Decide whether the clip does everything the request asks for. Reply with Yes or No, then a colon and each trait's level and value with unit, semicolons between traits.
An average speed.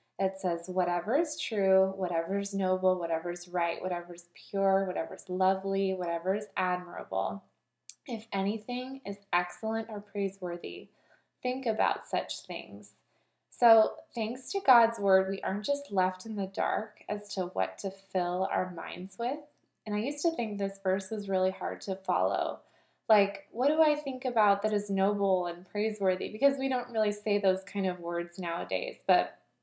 Yes: average, 170 wpm